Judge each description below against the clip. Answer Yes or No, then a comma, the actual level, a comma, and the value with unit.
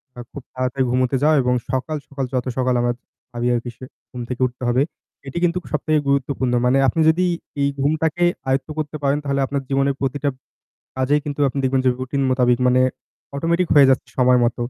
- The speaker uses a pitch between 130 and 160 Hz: Yes, low, 135 Hz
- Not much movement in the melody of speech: Yes, narrow, 2.3 semitones